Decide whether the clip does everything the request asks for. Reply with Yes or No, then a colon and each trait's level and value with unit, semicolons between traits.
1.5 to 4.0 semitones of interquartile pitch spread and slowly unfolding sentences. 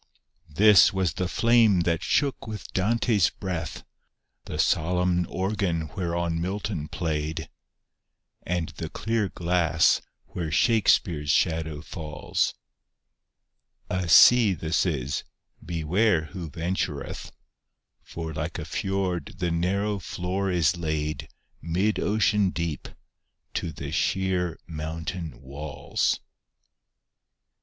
Yes: average, 3.3 semitones; slow, 105 wpm